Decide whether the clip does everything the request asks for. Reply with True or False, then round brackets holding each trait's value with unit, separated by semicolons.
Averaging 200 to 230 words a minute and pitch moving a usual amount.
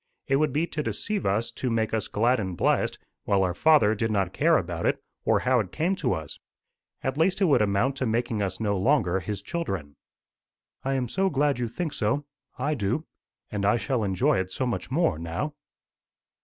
False (205 wpm; 6.7 semitones)